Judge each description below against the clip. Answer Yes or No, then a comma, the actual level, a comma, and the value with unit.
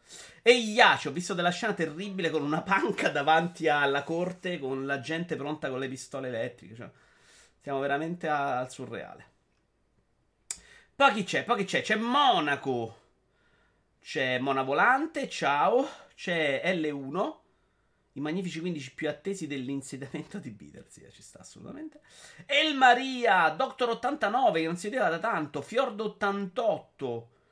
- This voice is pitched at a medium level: Yes, medium, 165 Hz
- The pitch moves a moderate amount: No, wide, 7.5 semitones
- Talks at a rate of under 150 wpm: Yes, average, 140 wpm